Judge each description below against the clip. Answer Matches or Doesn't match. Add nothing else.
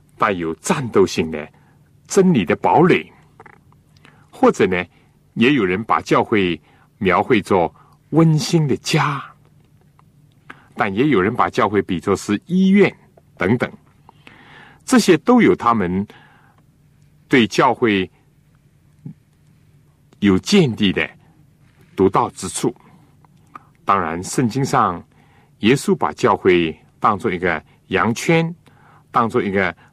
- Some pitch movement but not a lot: Doesn't match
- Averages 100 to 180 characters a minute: Matches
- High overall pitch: Doesn't match